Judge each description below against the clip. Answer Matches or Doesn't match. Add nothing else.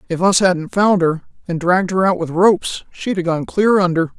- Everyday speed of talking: Doesn't match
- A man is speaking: Doesn't match